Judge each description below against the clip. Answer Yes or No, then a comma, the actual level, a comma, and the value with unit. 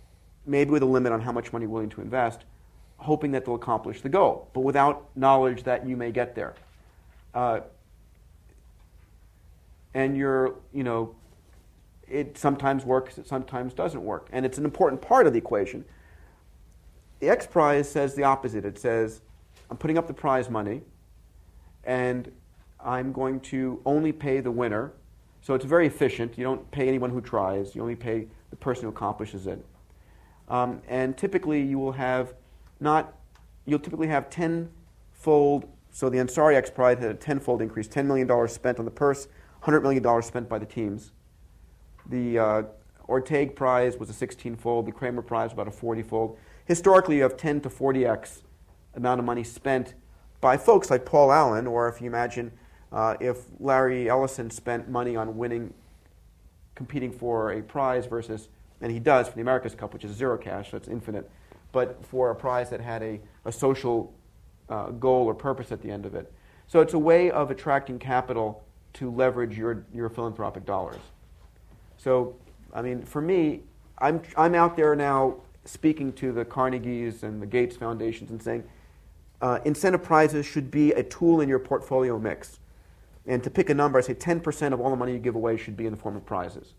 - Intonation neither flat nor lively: Yes, average, 3.7 semitones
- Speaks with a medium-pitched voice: No, low, 120 Hz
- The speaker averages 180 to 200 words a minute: Yes, average, 185 wpm